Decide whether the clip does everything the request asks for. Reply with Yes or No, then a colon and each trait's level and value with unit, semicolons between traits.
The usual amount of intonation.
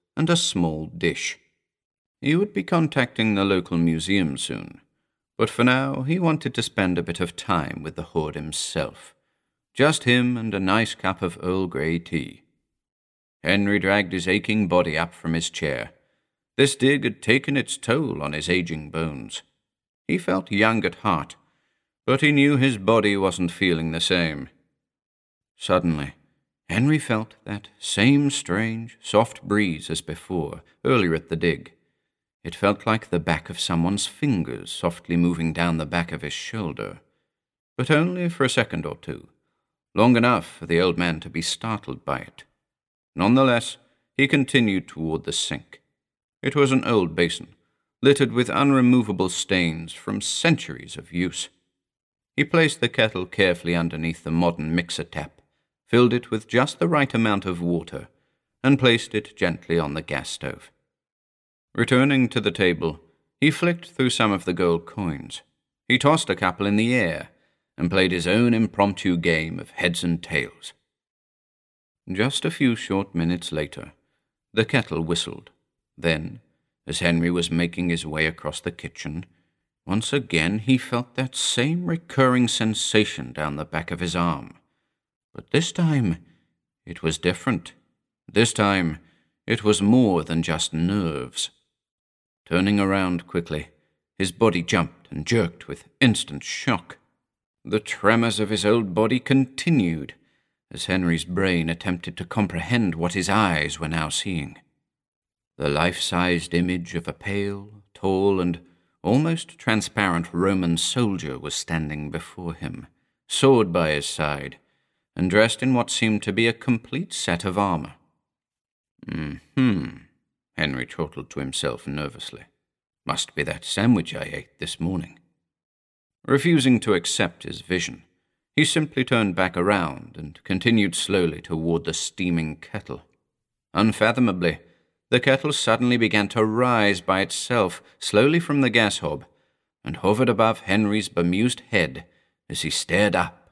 No: wide, 5.9 semitones